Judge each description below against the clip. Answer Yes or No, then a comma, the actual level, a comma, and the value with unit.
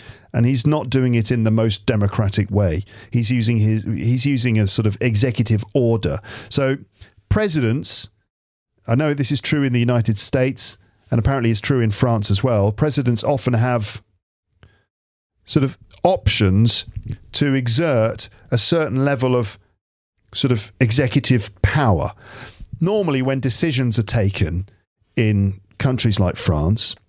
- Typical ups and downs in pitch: Yes, average, 4.0 semitones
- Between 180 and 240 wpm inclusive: No, average, 140 wpm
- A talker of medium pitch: No, low, 115 Hz